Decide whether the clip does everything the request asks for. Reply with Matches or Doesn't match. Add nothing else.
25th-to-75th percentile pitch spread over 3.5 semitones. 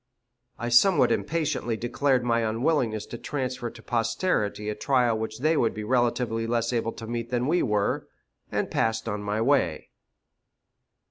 Doesn't match